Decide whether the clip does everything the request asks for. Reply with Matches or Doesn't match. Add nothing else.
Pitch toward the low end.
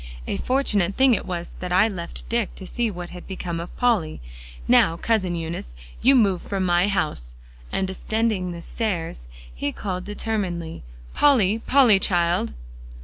Doesn't match